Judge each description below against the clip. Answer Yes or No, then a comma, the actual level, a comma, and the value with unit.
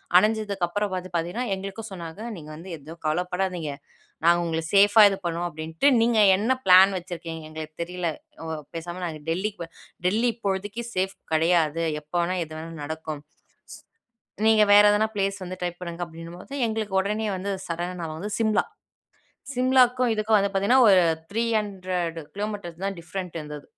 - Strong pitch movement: No, average, 3.8 semitones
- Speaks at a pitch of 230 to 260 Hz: No, medium, 185 Hz